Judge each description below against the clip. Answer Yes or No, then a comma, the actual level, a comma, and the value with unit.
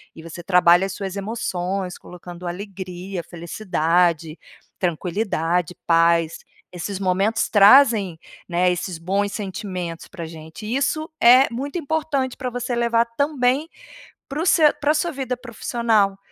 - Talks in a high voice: Yes, high, 195 Hz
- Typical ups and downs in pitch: No, wide, 5.7 semitones